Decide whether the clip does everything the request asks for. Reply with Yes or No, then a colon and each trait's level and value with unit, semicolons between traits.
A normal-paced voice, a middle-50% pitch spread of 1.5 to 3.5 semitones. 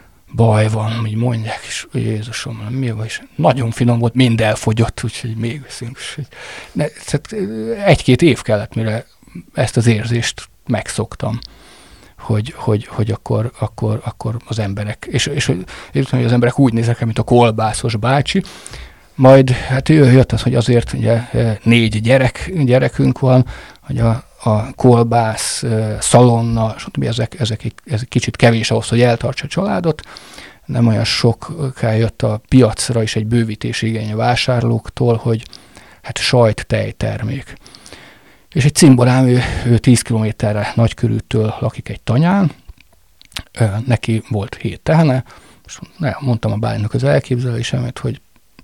Yes: average, 135 wpm; narrow, 2.4 semitones